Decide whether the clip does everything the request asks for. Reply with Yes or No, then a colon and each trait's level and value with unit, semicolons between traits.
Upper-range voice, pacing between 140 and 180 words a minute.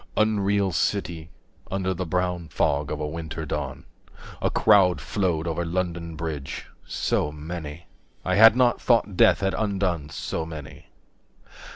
No: very low, 85 Hz; average, 145 wpm